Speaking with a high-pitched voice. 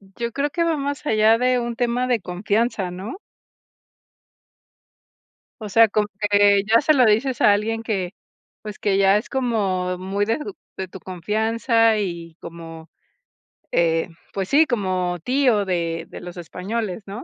Yes: high, 210 Hz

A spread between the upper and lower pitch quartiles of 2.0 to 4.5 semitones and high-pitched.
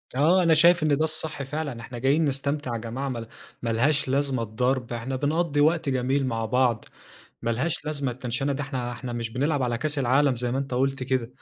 No: average, 3.2 semitones; low, 135 Hz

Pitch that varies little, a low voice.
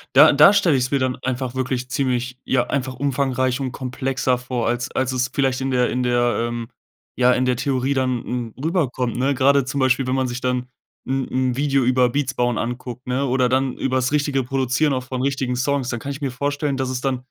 Yes: narrow, 1.4 semitones; low, 130 Hz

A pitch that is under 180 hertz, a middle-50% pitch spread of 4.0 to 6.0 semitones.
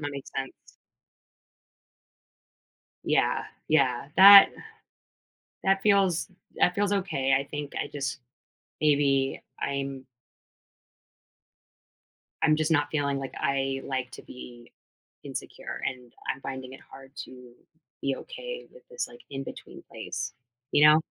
Yes: medium, 140 Hz; average, 4.3 semitones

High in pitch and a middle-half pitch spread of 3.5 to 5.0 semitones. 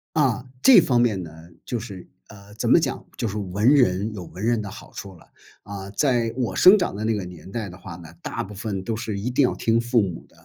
No: low, 105 Hz; average, 3.8 semitones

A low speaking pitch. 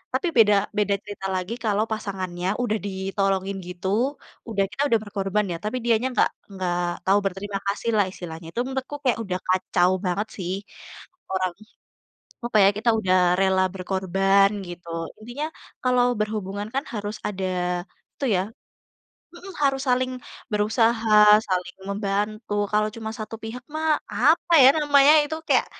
No: high, 205 Hz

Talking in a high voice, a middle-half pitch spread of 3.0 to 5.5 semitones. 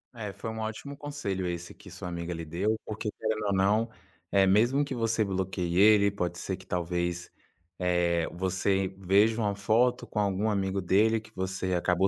No: very low, 95 Hz; average, 3.4 semitones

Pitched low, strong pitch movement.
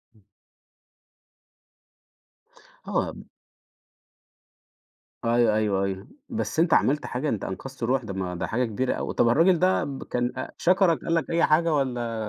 Yes: low, 125 Hz; wide, 6.3 semitones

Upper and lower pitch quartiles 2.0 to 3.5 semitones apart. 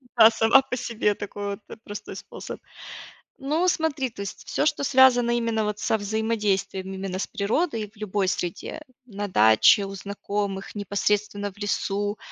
Yes: average, 2.9 semitones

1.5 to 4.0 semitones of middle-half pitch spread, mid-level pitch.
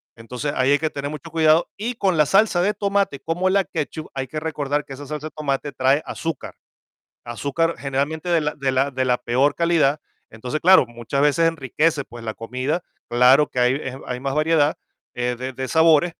Yes: average, 3.6 semitones; medium, 145 Hz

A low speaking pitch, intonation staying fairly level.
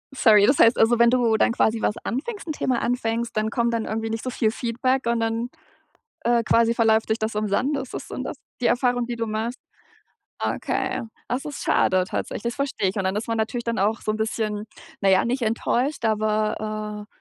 No: high, 230 Hz; narrow, 2.0 semitones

